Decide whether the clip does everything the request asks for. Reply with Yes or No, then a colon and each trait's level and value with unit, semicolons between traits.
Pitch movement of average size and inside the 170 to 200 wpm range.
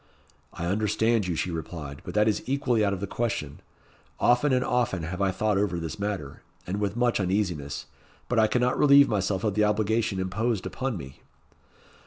Yes: average, 4.2 semitones; average, 185 wpm